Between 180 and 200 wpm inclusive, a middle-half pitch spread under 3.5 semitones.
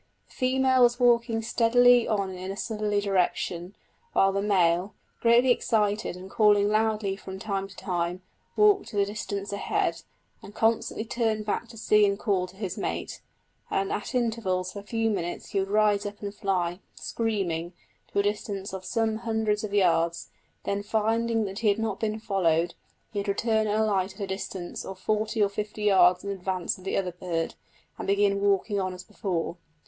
Yes: average, 185 wpm; narrow, 2.5 semitones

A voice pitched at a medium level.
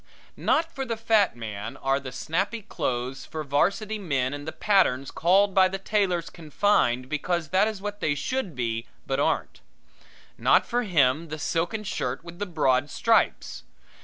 Yes: medium, 170 Hz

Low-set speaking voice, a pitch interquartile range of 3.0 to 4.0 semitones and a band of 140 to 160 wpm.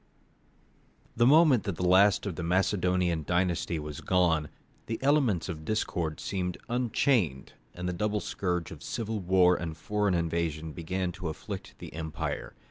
Yes: very low, 90 Hz; average, 3.7 semitones; average, 150 wpm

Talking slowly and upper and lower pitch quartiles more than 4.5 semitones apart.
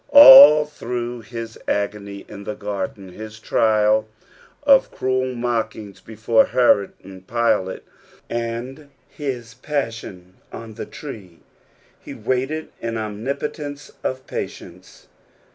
No: slow, 110 wpm; average, 3.7 semitones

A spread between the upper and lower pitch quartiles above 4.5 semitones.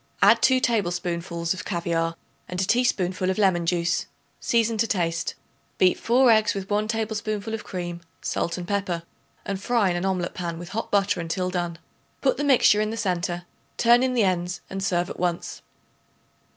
No: average, 3.8 semitones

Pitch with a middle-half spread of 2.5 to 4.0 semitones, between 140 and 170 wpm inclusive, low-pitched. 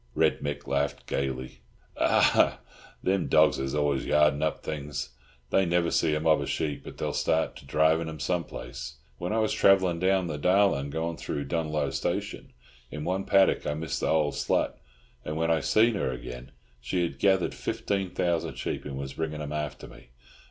No: average, 3.6 semitones; average, 185 wpm; very low, 80 Hz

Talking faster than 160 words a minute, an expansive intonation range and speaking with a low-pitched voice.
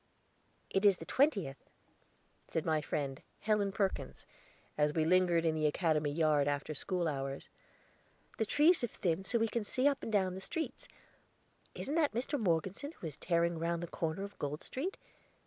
No: average, 175 wpm; wide, 5.7 semitones; medium, 175 Hz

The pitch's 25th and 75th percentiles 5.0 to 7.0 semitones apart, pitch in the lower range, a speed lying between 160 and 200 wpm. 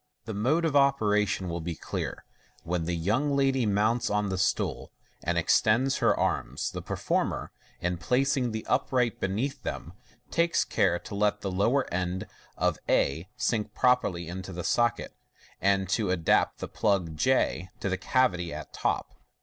Yes: wide, 5.6 semitones; low, 105 Hz; average, 165 wpm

